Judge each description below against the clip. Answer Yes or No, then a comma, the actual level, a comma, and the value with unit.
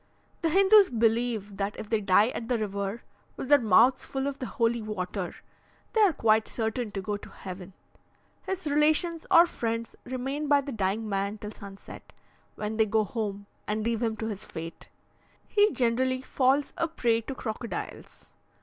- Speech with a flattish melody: No, average, 4.3 semitones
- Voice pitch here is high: Yes, high, 230 Hz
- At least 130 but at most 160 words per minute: No, average, 175 wpm